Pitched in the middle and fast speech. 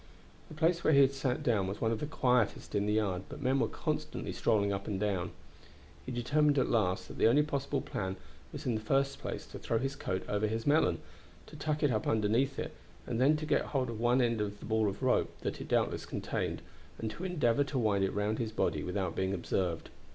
No: low, 115 Hz; fast, 230 wpm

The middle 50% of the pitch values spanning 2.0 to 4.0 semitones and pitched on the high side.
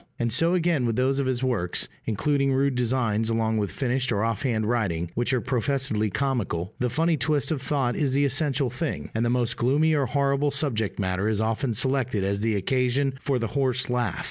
No: average, 3.6 semitones; low, 125 Hz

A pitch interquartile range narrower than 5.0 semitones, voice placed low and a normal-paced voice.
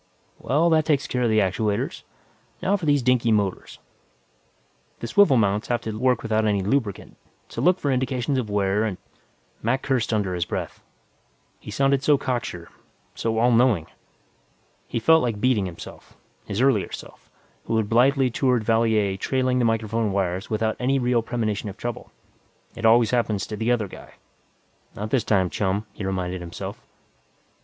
Yes: average, 3.6 semitones; low, 115 Hz; average, 170 wpm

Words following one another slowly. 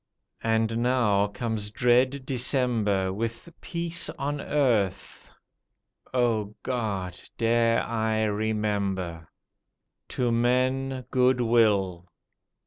Yes: slow, 80 wpm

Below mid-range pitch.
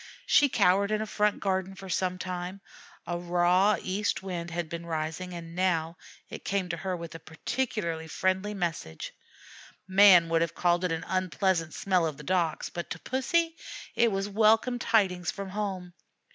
No: medium, 185 Hz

